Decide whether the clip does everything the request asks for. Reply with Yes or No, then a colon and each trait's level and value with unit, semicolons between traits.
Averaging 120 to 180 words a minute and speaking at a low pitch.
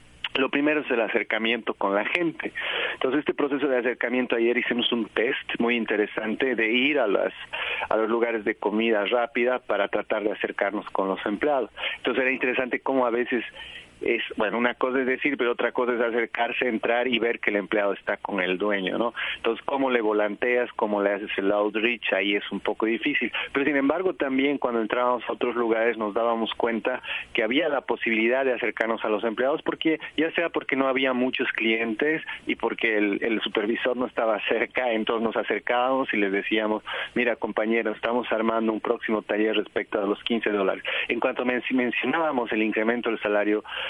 No: fast, 190 wpm; low, 115 Hz